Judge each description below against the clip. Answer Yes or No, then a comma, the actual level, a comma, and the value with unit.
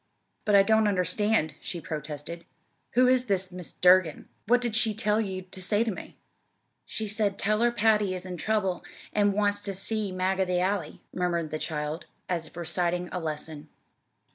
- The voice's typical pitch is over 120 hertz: Yes, high, 190 Hz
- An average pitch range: Yes, average, 3.4 semitones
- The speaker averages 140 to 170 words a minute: No, average, 185 wpm